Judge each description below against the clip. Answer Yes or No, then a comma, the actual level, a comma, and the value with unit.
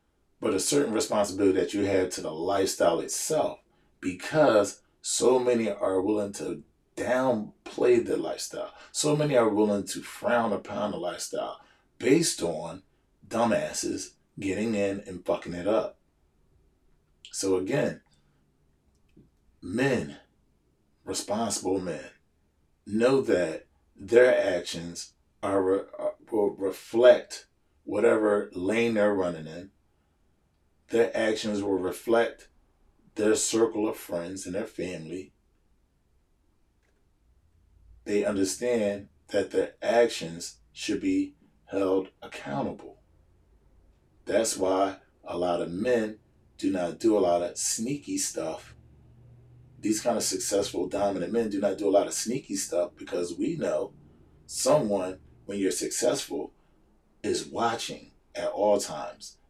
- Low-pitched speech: Yes, very low, 95 Hz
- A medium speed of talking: No, slow, 115 wpm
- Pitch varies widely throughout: Yes, wide, 5.8 semitones